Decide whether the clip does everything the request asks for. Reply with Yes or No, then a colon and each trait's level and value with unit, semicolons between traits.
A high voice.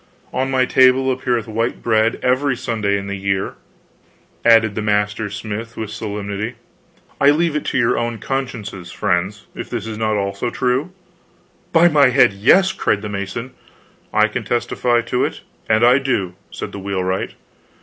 No: low, 115 Hz